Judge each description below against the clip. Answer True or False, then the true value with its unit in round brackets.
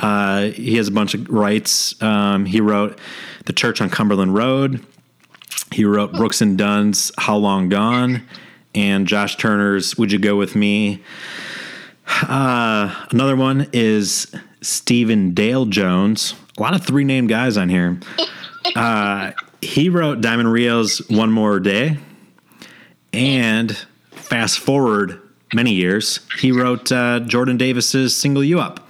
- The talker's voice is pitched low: True (110 Hz)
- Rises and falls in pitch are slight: False (3.5 semitones)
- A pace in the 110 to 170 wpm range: True (140 wpm)